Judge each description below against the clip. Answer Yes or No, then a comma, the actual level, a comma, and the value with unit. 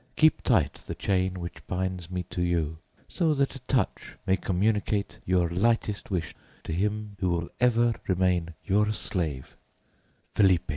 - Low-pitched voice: Yes, very low, 95 Hz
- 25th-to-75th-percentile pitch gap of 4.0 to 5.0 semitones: No, average, 3.3 semitones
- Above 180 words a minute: No, average, 150 wpm